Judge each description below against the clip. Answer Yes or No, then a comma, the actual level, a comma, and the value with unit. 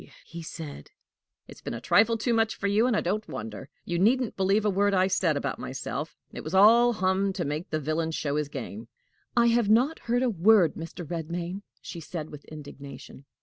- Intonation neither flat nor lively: No, wide, 5.7 semitones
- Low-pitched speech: No, medium, 185 Hz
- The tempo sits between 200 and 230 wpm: Yes, fast, 205 wpm